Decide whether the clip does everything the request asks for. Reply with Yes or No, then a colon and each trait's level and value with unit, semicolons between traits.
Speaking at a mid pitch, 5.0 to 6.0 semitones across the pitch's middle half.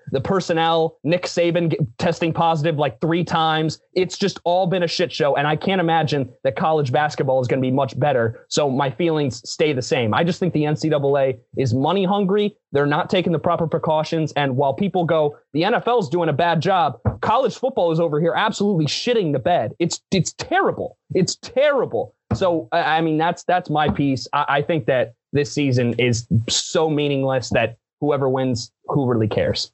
No: medium, 160 Hz; average, 3.8 semitones